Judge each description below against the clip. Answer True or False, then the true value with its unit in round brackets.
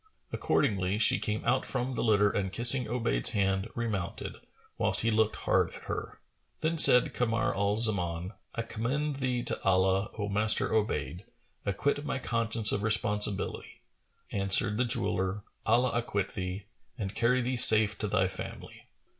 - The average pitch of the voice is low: True (110 Hz)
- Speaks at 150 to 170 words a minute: True (155 wpm)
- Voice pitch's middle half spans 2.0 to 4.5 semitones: True (3.3 semitones)